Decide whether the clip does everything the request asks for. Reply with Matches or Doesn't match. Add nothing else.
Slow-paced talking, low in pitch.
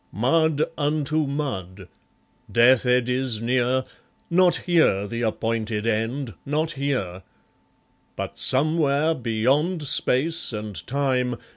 Matches